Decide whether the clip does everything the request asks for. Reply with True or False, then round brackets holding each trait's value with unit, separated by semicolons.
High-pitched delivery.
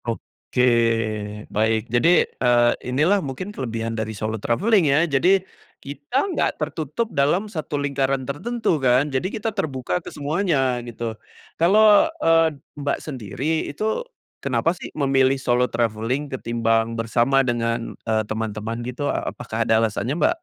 False (135 Hz)